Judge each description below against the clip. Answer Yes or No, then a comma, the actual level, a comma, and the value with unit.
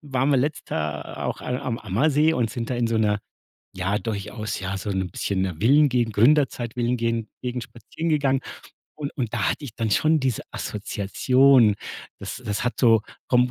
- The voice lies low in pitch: Yes, low, 120 Hz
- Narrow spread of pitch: No, average, 4.1 semitones